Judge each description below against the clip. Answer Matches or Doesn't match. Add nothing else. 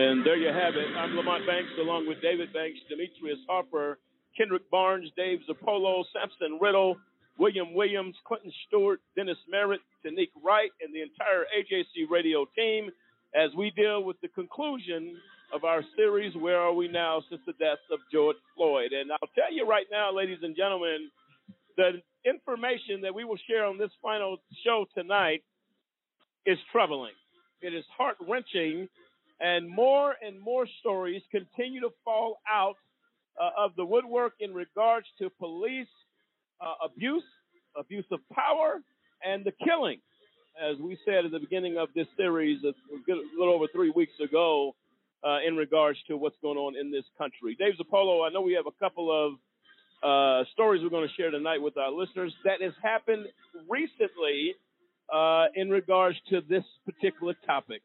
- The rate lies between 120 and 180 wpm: Matches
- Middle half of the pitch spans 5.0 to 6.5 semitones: Matches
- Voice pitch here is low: Doesn't match